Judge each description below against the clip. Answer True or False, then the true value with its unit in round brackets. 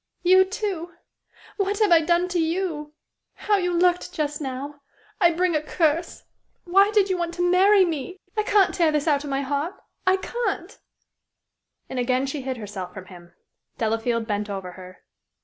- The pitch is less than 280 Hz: False (330 Hz)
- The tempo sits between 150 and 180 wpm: True (175 wpm)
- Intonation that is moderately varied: False (5.7 semitones)